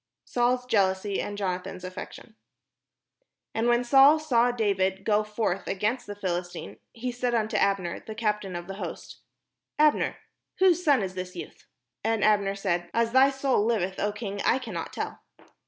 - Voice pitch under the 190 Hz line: No, high, 210 Hz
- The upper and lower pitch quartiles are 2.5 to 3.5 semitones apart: No, average, 4.2 semitones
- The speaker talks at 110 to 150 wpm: No, average, 170 wpm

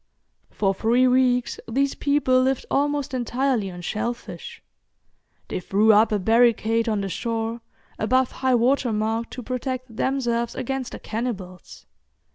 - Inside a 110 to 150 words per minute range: Yes, slow, 135 wpm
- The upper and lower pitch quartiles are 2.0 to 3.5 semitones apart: Yes, average, 2.7 semitones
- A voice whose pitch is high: Yes, high, 235 Hz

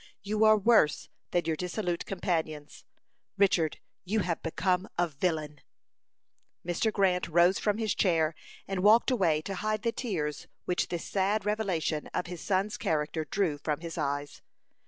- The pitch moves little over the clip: No, average, 4.3 semitones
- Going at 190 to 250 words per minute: No, average, 155 wpm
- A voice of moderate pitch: Yes, medium, 180 Hz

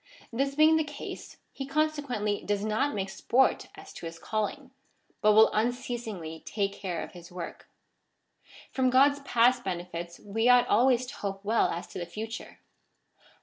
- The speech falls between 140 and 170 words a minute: Yes, average, 160 wpm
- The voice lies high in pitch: Yes, high, 225 Hz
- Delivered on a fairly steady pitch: No, average, 5.0 semitones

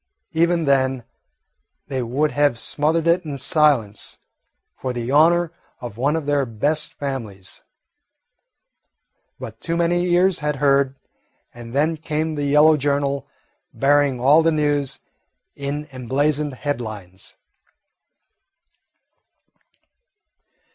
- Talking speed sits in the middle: No, slow, 105 wpm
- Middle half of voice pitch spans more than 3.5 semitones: No, average, 2.7 semitones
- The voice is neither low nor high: Yes, medium, 145 Hz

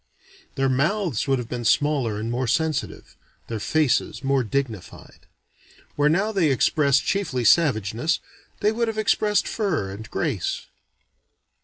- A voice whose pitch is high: No, medium, 140 Hz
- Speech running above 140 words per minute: No, slow, 135 wpm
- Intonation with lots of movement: Yes, wide, 6.1 semitones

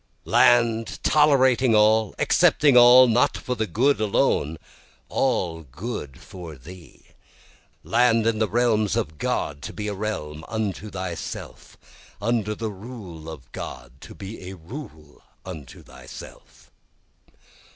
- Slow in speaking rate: Yes, slow, 130 wpm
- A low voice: Yes, low, 105 Hz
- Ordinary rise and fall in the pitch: No, wide, 5.9 semitones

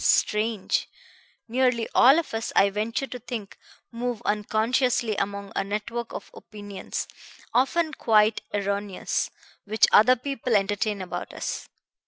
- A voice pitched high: Yes, high, 220 Hz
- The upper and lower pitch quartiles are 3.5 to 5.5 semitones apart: No, average, 3.1 semitones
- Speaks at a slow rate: Yes, slow, 125 wpm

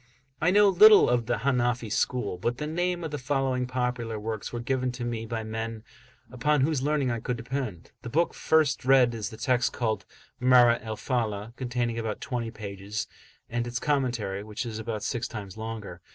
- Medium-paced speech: Yes, average, 195 wpm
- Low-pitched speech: Yes, low, 120 Hz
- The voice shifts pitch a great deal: No, average, 2.9 semitones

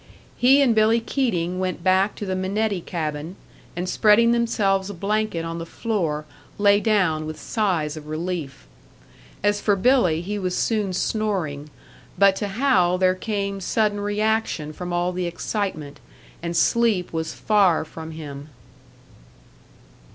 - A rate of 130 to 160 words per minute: Yes, average, 145 wpm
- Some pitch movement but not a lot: Yes, average, 4.2 semitones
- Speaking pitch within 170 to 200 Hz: Yes, high, 190 Hz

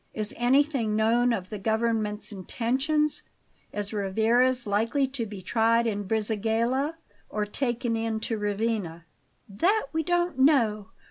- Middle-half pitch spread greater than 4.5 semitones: No, average, 3.6 semitones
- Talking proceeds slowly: Yes, slow, 130 wpm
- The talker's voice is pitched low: No, high, 225 Hz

